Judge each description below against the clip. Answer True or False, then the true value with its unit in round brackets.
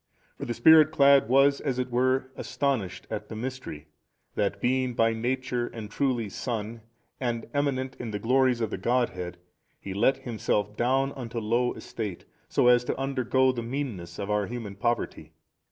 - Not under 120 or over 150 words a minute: False (170 wpm)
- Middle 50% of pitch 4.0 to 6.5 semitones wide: False (3.3 semitones)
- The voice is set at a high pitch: False (120 Hz)